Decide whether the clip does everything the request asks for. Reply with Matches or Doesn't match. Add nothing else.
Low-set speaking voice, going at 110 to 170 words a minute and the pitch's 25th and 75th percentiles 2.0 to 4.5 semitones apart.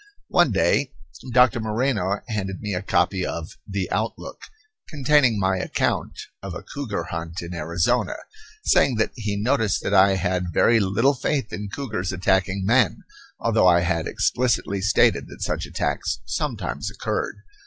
Matches